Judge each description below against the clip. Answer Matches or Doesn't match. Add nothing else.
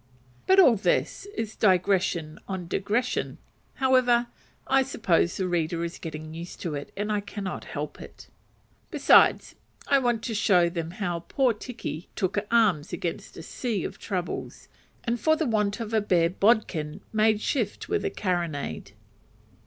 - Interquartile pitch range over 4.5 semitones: Matches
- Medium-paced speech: Matches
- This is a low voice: Doesn't match